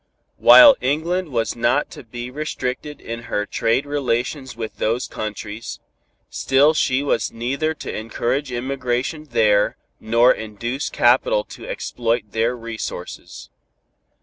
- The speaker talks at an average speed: No, slow, 120 wpm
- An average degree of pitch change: Yes, average, 3.9 semitones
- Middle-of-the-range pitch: No, low, 125 Hz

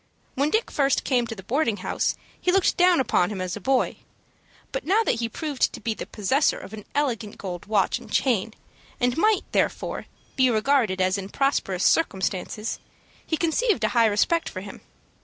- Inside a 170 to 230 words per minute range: Yes, average, 190 wpm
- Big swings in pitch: Yes, wide, 6.4 semitones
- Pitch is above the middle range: Yes, high, 240 Hz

